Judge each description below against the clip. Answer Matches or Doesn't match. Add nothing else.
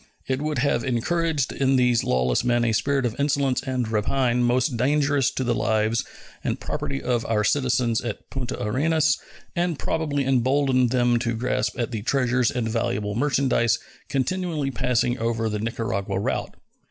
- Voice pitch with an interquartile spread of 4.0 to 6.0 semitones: Doesn't match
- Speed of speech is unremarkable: Matches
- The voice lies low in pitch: Matches